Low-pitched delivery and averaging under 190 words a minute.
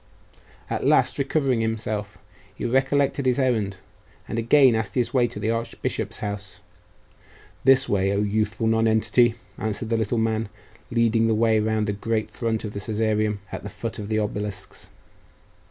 Yes: low, 110 Hz; average, 160 wpm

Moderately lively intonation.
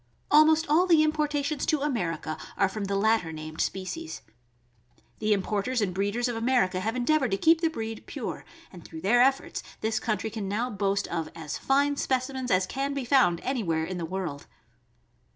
No: wide, 6.4 semitones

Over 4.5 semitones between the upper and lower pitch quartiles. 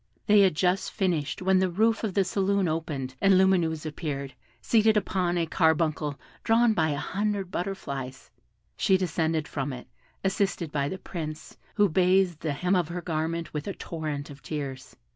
No: average, 4.0 semitones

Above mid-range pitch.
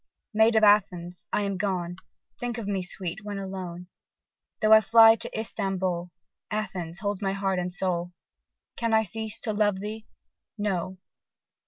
Yes: high, 195 Hz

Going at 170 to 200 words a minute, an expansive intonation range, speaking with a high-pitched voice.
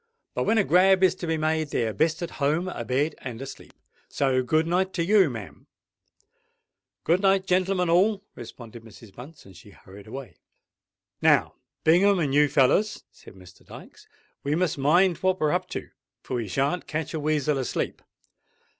No: average, 175 wpm; wide, 5.9 semitones; medium, 155 Hz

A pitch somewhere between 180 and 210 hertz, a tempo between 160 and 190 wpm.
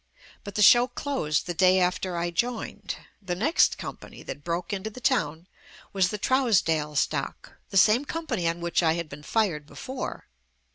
Yes: medium, 185 Hz; average, 180 wpm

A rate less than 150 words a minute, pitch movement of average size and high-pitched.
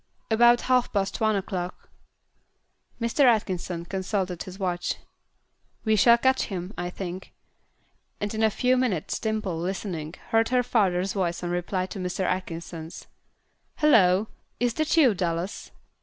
Yes: average, 140 wpm; average, 4.1 semitones; high, 195 Hz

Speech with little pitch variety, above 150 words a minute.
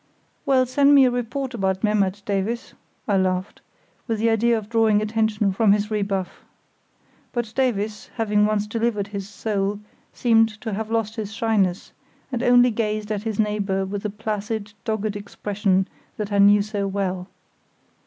Yes: narrow, 2.0 semitones; average, 160 wpm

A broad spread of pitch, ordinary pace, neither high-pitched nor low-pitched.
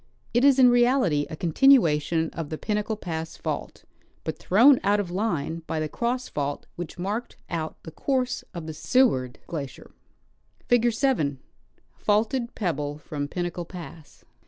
Yes: wide, 7.4 semitones; average, 155 wpm; medium, 175 Hz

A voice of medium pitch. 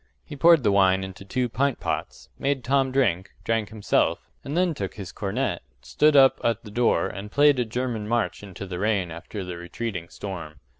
No: low, 110 Hz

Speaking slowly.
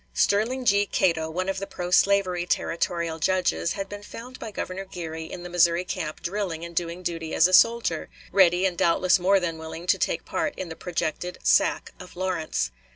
No: average, 195 wpm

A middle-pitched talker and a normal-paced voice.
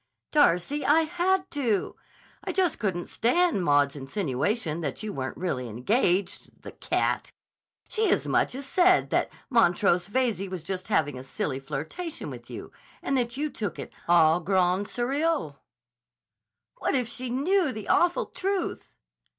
No: high, 210 Hz; average, 145 wpm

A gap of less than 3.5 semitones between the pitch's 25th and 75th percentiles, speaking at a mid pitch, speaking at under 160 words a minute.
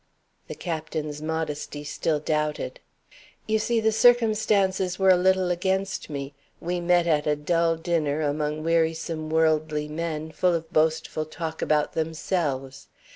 Yes: average, 2.8 semitones; medium, 160 Hz; slow, 135 wpm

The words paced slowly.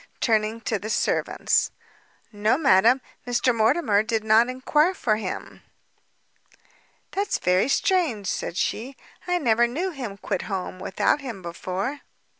Yes: slow, 130 wpm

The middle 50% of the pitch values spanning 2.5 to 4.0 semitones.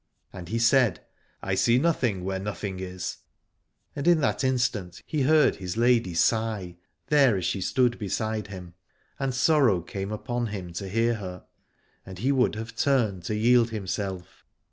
No: average, 4.7 semitones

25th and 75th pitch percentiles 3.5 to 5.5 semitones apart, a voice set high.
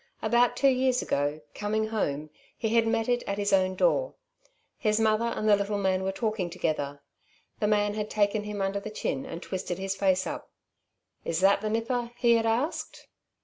No: average, 3.0 semitones; high, 210 Hz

